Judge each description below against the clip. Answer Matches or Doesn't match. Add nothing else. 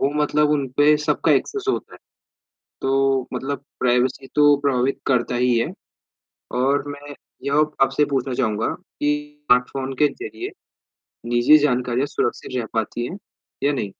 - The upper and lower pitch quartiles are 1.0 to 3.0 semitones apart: Matches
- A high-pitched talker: Doesn't match